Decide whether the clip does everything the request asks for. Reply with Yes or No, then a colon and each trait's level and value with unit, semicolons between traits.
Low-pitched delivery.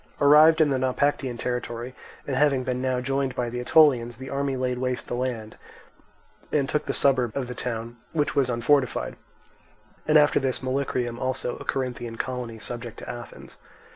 Yes: low, 130 Hz